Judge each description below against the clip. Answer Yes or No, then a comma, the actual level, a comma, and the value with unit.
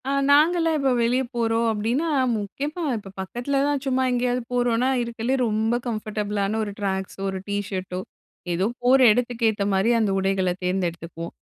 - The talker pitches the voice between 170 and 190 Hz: No, high, 225 Hz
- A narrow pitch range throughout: No, average, 4.3 semitones